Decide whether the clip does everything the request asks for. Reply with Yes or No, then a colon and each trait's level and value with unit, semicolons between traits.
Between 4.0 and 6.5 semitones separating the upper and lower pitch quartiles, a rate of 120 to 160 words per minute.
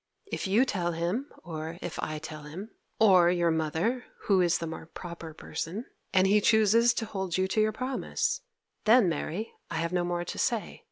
No: average, 4.7 semitones; average, 190 wpm